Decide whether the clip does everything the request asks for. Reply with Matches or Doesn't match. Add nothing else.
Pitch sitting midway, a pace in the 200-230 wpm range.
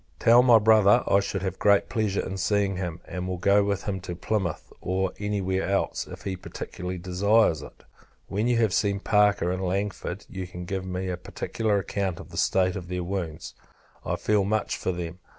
Doesn't match